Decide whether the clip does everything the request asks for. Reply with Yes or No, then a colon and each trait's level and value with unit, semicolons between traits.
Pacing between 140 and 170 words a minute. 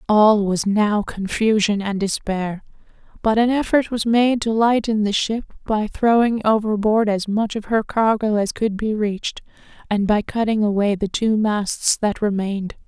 Yes: average, 165 wpm